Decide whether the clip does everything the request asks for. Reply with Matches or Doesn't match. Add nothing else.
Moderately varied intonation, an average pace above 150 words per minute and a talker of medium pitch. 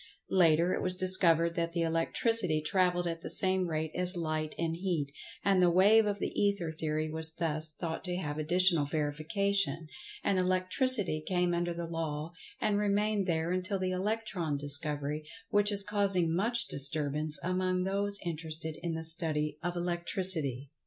Matches